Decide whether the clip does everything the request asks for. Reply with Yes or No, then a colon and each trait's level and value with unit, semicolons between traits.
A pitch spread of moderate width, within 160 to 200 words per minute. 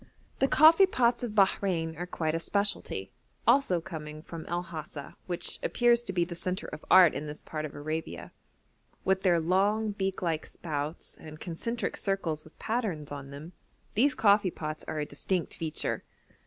Yes: average, 4.5 semitones; average, 170 wpm